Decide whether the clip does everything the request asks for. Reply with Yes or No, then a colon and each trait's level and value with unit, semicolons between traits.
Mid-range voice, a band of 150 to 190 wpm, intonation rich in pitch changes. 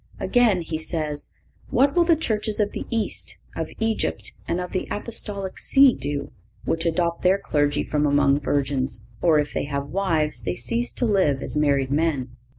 Yes: medium, 155 Hz; average, 180 wpm; wide, 5.9 semitones